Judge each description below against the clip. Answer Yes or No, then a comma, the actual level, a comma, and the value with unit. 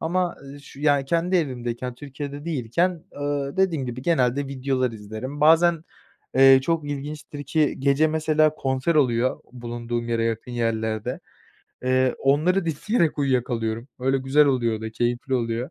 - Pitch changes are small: No, average, 4.0 semitones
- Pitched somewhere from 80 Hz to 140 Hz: Yes, low, 135 Hz